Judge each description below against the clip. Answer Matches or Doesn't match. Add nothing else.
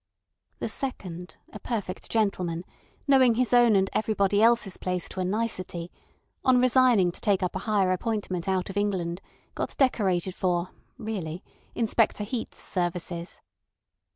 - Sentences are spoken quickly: Doesn't match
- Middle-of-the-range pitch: Doesn't match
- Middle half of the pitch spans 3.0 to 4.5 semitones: Matches